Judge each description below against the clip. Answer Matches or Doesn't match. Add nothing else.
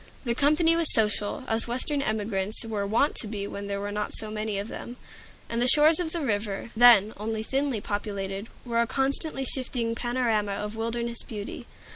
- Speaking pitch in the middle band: Doesn't match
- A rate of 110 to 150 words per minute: Doesn't match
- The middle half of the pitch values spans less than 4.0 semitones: Matches